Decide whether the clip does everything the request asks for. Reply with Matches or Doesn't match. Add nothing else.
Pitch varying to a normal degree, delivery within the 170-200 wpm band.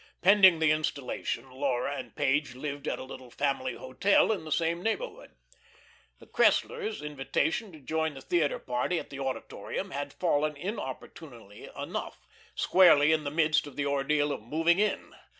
Doesn't match